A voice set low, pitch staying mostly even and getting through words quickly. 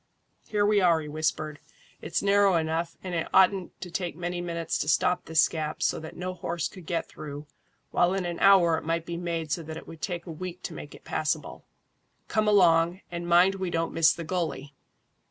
No: medium, 170 Hz; narrow, 2.2 semitones; fast, 210 wpm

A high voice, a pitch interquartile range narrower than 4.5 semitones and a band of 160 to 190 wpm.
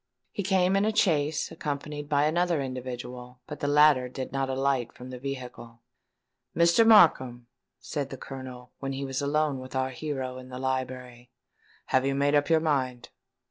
No: low, 135 Hz; average, 2.7 semitones; average, 175 wpm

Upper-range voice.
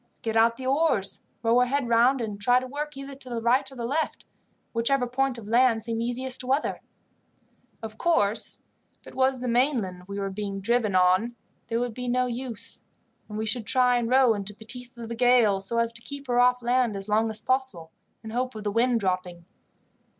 Yes: high, 235 Hz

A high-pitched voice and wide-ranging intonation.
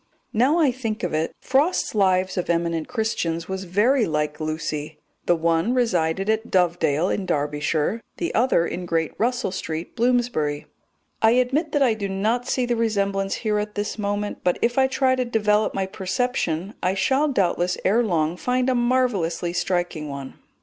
Yes: high, 200 Hz; wide, 6.2 semitones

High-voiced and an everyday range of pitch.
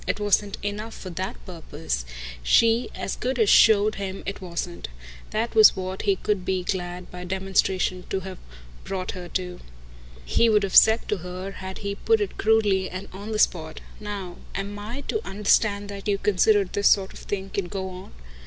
No: high, 195 Hz; narrow, 2.2 semitones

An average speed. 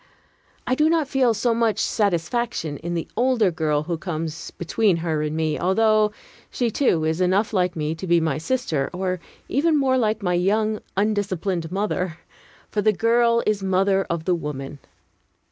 Yes: average, 170 wpm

